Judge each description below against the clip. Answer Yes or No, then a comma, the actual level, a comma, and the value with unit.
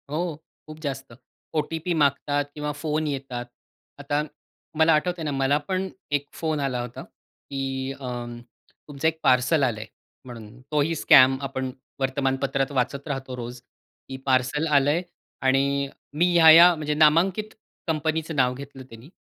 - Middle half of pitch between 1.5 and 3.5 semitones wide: Yes, average, 2.9 semitones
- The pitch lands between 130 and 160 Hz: Yes, medium, 140 Hz